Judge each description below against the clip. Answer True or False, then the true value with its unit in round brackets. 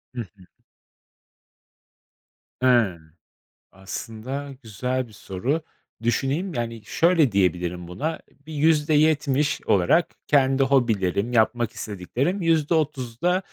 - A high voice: False (130 Hz)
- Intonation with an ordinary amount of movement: False (5.8 semitones)